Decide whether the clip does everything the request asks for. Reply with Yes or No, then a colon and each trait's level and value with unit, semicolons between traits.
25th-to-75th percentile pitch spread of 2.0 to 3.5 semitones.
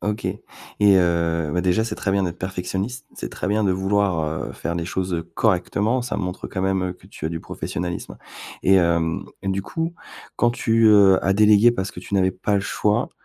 Yes: narrow, 2.6 semitones